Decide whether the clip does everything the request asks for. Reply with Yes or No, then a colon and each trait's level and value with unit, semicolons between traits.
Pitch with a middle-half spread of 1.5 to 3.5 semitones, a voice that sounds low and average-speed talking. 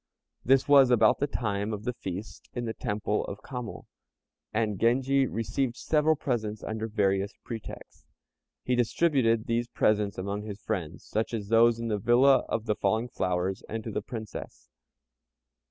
Yes: average, 2.8 semitones; low, 110 Hz; average, 160 wpm